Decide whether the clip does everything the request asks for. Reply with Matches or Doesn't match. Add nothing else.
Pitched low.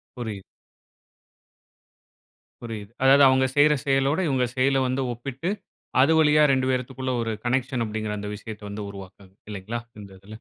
Matches